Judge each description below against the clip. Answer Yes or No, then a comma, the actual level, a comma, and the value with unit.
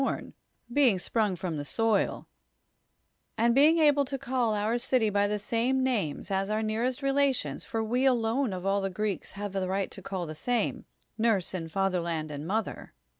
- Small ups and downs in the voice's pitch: No, average, 4.5 semitones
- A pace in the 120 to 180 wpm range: No, average, 190 wpm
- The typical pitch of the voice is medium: No, high, 215 Hz